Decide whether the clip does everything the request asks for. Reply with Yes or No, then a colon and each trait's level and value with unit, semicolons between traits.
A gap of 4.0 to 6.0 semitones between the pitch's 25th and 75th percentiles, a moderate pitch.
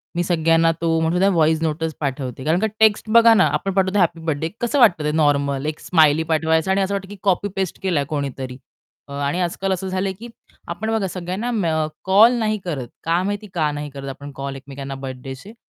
Yes: average, 5.0 semitones; medium, 165 Hz